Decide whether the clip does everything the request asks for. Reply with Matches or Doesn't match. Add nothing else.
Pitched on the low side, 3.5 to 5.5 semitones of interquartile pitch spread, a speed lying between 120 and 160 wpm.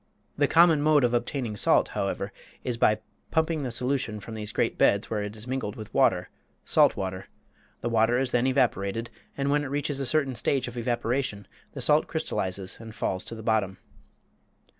Doesn't match